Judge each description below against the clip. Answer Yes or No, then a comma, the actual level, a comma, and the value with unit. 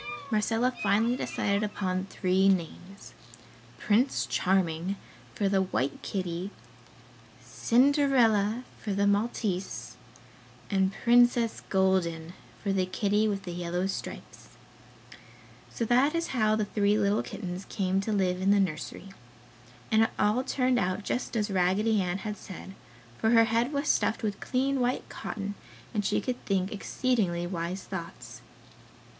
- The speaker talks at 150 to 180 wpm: No, average, 140 wpm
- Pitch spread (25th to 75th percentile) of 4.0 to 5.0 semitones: No, average, 3.2 semitones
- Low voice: No, high, 200 Hz